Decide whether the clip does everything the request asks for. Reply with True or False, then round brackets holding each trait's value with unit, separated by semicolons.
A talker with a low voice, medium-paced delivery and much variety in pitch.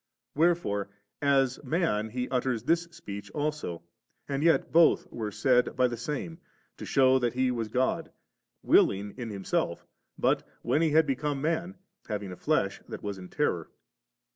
True (130 Hz; 165 wpm; 5.8 semitones)